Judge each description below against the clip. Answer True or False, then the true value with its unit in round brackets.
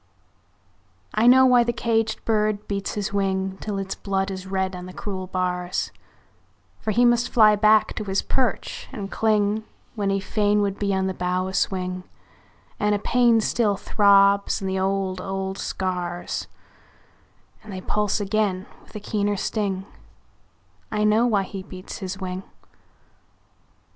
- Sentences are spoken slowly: False (160 wpm)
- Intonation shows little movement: True (2.1 semitones)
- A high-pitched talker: True (200 Hz)